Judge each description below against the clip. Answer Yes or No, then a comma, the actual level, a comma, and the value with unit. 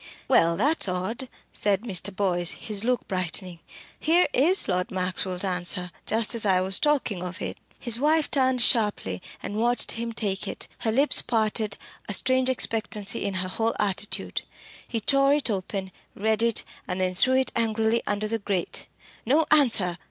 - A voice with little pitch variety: No, average, 4.5 semitones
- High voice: Yes, high, 215 Hz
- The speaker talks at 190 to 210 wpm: No, average, 165 wpm